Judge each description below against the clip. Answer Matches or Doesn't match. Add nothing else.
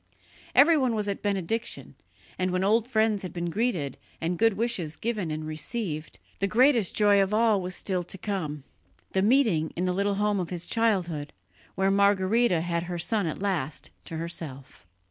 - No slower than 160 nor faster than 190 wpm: Matches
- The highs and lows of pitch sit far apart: Doesn't match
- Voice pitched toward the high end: Matches